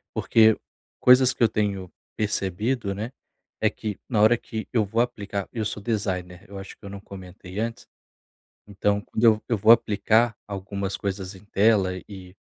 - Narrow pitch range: Yes, narrow, 2.3 semitones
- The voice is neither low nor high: No, low, 105 Hz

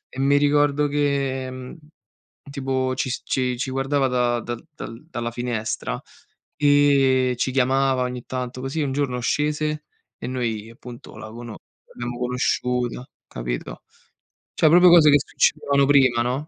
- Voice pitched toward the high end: No, low, 130 Hz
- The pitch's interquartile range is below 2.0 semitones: No, narrow, 2.5 semitones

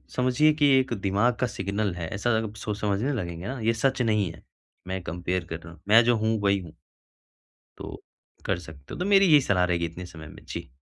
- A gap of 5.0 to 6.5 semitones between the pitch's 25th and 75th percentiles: Yes, wide, 5.6 semitones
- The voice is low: Yes, low, 100 Hz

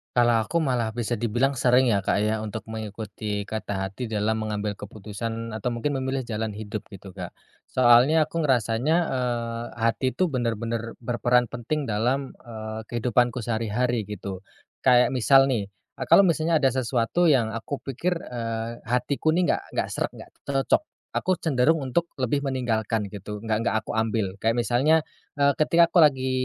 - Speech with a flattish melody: No, average, 3.3 semitones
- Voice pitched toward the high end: No, low, 120 Hz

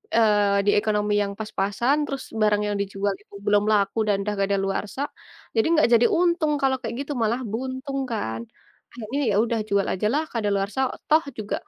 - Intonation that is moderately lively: Yes, average, 4.4 semitones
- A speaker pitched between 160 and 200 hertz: No, high, 215 Hz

